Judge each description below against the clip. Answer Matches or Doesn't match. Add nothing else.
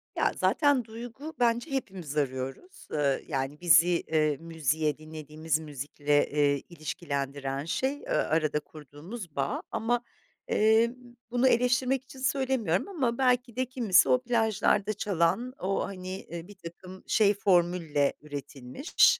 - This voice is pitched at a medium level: Matches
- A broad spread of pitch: Matches